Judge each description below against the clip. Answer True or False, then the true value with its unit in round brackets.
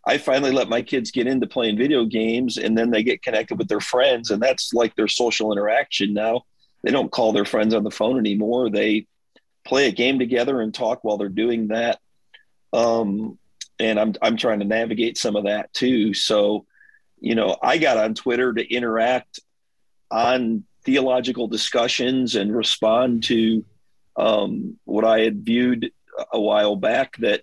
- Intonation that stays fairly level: True (2.3 semitones)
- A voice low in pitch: True (115 Hz)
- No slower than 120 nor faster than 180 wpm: True (175 wpm)